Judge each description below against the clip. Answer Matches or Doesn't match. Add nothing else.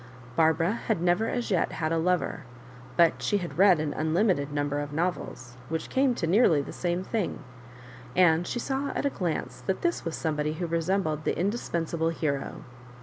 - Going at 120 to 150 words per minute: Doesn't match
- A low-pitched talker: Doesn't match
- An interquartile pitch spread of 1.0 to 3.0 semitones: Doesn't match